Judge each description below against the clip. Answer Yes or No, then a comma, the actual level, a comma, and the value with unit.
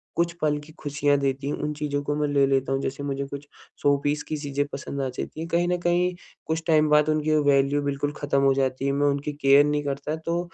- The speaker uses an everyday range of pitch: No, narrow, 1.6 semitones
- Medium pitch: Yes, medium, 145 Hz